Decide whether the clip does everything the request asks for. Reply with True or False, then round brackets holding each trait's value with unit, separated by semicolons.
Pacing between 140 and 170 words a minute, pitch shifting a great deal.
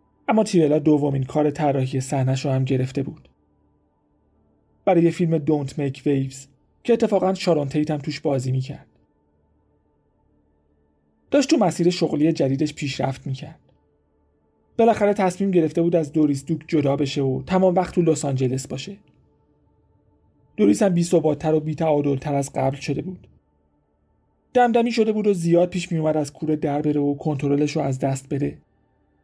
True (150 wpm; 8.7 semitones)